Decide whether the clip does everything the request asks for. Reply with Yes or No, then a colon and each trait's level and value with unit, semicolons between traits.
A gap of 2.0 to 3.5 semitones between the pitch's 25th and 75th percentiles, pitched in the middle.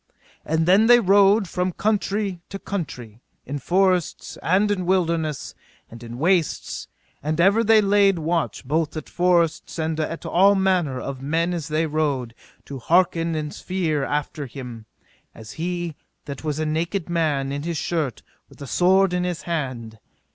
No: average, 4.0 semitones; medium, 165 Hz